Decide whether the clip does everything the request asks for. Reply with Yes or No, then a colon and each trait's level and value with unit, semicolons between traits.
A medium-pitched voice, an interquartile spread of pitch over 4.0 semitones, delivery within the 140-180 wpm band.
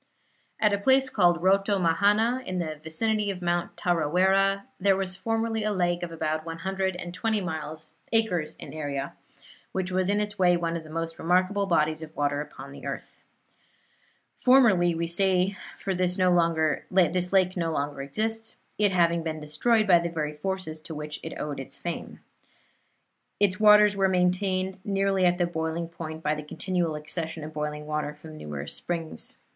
No: medium, 175 Hz; average, 3.5 semitones; average, 170 wpm